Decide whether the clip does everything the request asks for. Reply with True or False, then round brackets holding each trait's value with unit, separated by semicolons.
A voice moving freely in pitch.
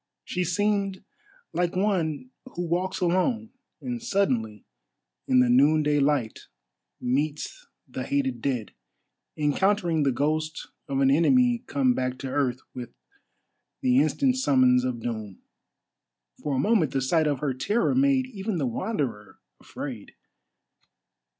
True (8.1 semitones)